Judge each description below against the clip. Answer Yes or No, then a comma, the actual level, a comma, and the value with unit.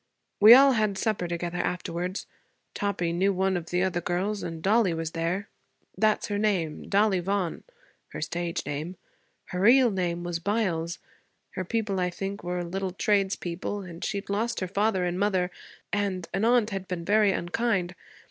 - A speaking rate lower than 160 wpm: No, average, 165 wpm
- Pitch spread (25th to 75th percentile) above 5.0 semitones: No, average, 2.8 semitones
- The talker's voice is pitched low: No, high, 190 Hz